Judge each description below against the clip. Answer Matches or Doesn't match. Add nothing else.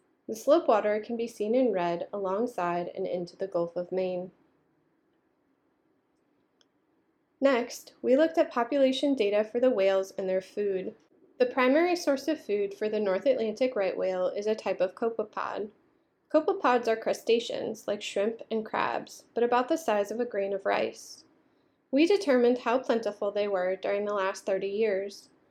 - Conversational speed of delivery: Matches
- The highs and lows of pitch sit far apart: Matches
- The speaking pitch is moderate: Doesn't match